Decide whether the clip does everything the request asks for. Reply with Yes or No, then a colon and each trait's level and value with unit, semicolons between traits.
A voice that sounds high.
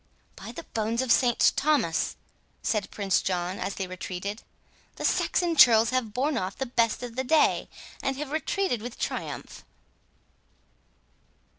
Yes: high, 235 Hz